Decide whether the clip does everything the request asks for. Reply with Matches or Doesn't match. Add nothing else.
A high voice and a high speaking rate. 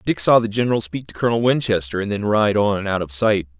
Doesn't match